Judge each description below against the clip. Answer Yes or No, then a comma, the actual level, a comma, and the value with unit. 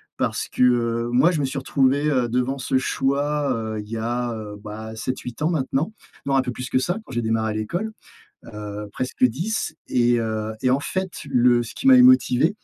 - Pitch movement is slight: No, average, 3.7 semitones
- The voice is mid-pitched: No, low, 125 Hz